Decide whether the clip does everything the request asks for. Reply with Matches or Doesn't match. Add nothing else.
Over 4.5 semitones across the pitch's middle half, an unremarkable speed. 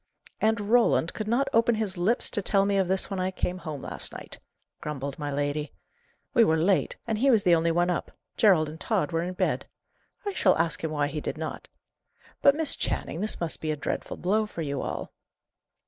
Doesn't match